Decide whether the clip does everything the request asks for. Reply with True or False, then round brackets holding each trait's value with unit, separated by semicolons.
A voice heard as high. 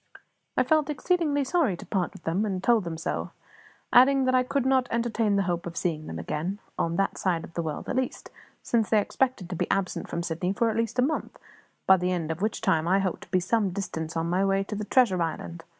True (195 Hz)